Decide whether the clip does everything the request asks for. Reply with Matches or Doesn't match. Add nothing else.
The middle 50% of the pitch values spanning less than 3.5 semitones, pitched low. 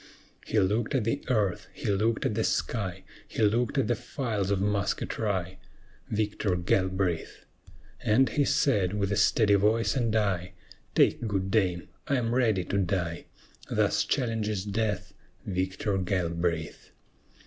Matches